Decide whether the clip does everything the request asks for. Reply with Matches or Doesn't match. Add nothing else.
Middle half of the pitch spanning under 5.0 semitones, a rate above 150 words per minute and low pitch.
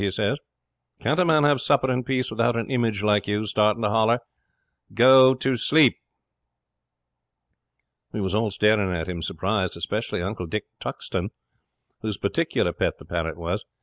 Matches